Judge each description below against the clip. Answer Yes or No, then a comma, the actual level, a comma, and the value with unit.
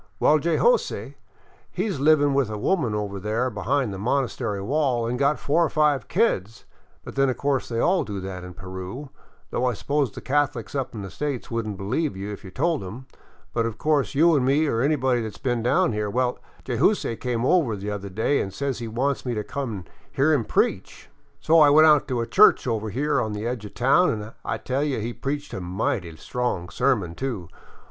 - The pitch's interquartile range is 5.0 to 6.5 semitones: Yes, average, 5.3 semitones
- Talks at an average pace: No, fast, 225 wpm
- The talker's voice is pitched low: Yes, low, 125 Hz